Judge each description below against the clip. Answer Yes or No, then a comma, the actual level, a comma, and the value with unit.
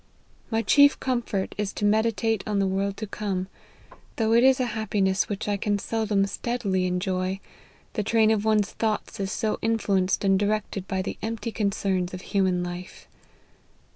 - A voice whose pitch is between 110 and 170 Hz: No, high, 205 Hz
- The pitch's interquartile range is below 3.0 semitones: Yes, narrow, 2.5 semitones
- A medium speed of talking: Yes, average, 170 wpm